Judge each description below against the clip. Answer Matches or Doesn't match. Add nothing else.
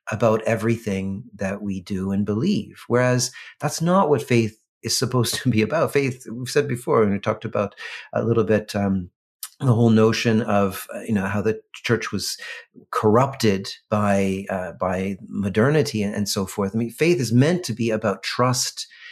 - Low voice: Matches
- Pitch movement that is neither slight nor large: Matches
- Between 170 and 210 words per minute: Matches